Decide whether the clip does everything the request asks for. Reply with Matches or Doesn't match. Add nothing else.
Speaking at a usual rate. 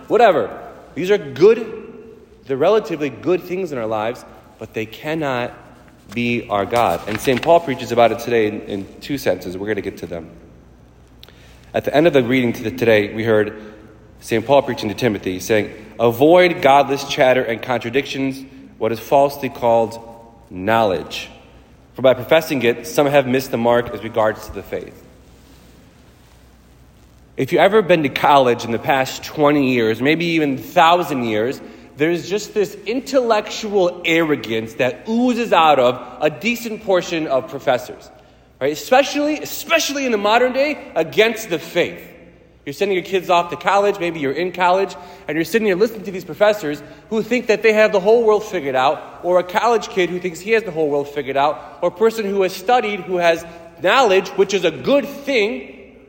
Matches